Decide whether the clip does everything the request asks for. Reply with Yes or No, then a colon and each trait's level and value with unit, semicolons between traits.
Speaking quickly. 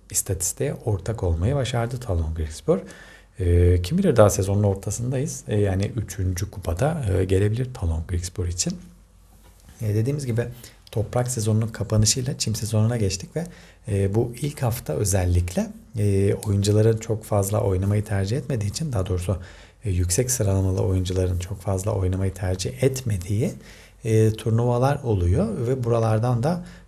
No: average, 120 wpm